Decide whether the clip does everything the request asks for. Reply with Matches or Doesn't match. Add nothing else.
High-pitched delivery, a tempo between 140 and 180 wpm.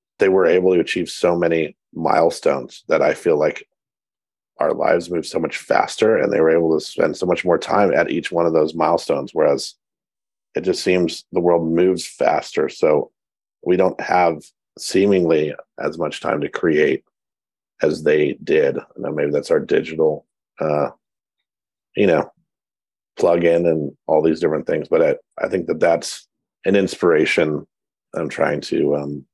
Doesn't match